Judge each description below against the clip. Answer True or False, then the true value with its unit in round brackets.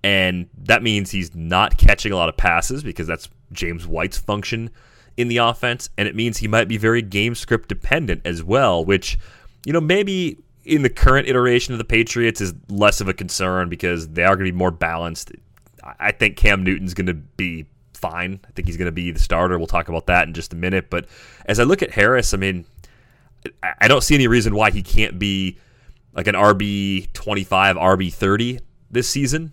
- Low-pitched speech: True (100 Hz)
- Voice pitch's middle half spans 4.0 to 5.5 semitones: True (4.4 semitones)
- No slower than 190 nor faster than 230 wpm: True (205 wpm)